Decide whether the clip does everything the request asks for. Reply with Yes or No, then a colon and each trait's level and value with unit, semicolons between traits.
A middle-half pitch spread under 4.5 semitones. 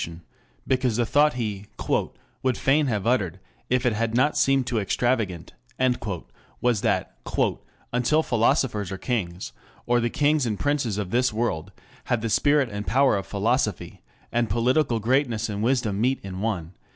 Yes: average, 4.0 semitones